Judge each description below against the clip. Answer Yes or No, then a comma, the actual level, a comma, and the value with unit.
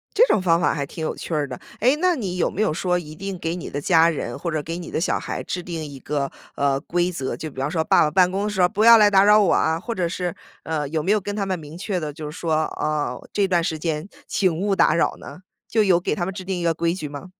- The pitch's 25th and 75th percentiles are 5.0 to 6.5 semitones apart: No, average, 3.6 semitones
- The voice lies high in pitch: No, medium, 175 Hz